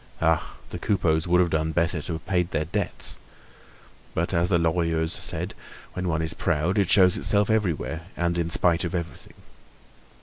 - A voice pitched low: Yes, very low, 85 Hz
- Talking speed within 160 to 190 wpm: Yes, average, 175 wpm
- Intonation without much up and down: Yes, narrow, 2.0 semitones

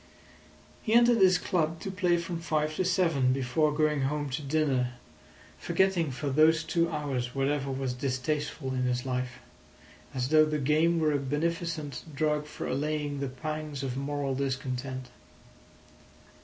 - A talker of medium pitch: Yes, medium, 150 Hz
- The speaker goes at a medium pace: Yes, average, 150 wpm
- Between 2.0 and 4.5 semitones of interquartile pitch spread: Yes, average, 3.1 semitones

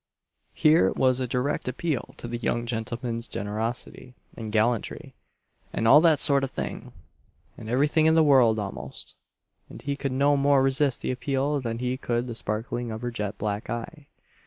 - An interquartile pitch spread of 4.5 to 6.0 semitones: No, average, 3.5 semitones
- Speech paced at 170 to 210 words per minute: Yes, average, 175 wpm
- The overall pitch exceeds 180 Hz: No, low, 125 Hz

